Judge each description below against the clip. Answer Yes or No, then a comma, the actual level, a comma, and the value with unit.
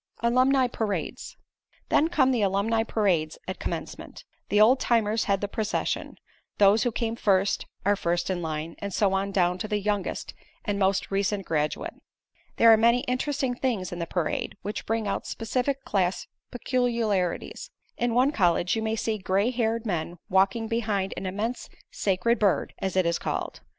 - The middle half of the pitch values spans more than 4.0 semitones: No, average, 3.4 semitones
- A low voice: No, high, 210 Hz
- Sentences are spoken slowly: No, average, 170 wpm